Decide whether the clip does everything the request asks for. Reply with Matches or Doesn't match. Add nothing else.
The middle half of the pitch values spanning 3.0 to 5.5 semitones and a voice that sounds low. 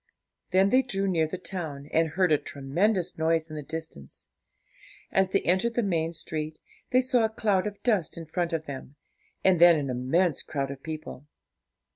Doesn't match